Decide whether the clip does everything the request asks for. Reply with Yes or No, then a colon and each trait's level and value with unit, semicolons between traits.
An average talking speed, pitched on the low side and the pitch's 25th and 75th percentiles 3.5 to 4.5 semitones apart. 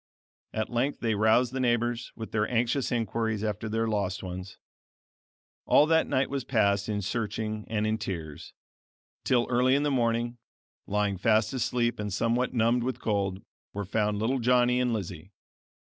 No: average, 160 wpm; low, 115 Hz; average, 2.7 semitones